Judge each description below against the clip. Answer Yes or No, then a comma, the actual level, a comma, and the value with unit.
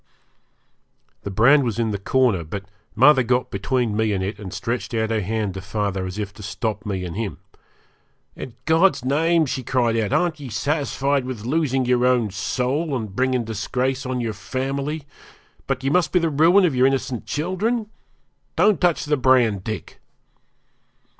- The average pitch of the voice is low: Yes, low, 125 Hz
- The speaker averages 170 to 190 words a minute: Yes, average, 175 wpm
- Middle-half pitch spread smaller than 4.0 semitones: No, average, 4.8 semitones